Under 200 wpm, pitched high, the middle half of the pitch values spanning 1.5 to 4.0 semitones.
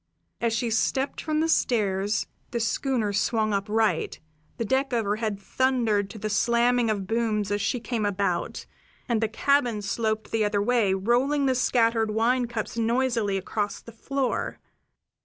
Yes: average, 155 wpm; high, 225 Hz; average, 2.9 semitones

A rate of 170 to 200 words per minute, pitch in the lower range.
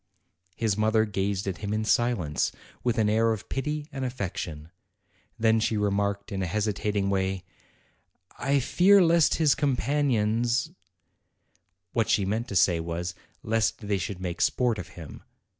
No: average, 160 wpm; low, 105 Hz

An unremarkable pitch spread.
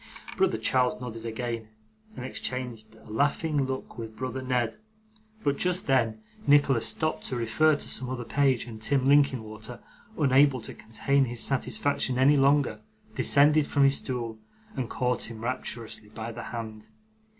Yes: average, 3.6 semitones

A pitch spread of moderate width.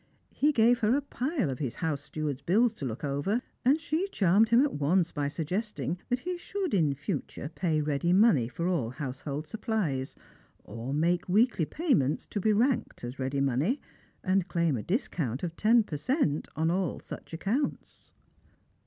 No: wide, 8.4 semitones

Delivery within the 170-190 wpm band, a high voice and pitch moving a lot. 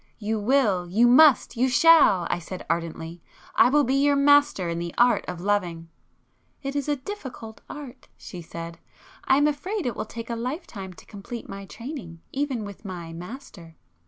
Yes: average, 180 wpm; high, 230 Hz; wide, 7.7 semitones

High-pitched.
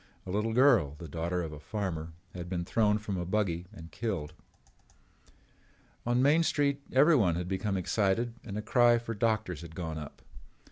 No: low, 100 Hz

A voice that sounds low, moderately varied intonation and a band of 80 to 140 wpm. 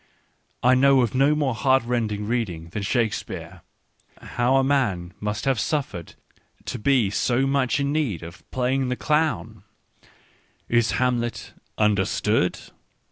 Yes: low, 125 Hz; average, 4.2 semitones; slow, 135 wpm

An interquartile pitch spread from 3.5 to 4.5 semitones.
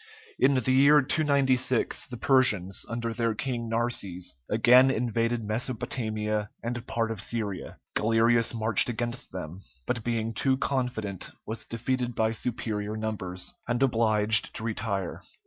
No: narrow, 2.5 semitones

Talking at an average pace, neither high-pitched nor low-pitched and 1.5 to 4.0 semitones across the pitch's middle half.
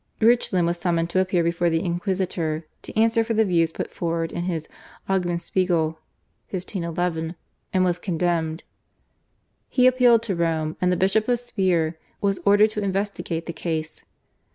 Yes: average, 155 wpm; medium, 175 Hz; average, 3.0 semitones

